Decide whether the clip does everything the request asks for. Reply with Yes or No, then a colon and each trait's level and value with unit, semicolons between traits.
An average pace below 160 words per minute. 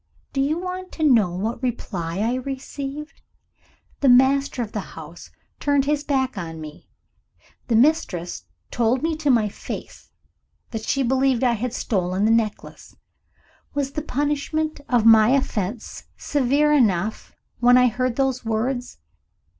Yes: average, 145 wpm